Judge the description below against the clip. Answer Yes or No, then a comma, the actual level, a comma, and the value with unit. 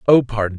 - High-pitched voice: No, low, 115 Hz